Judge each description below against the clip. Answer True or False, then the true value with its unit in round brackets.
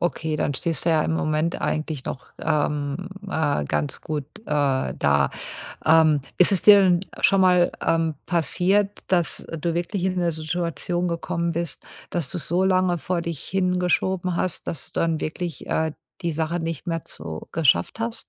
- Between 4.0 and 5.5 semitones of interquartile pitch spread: False (2.7 semitones)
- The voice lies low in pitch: False (165 Hz)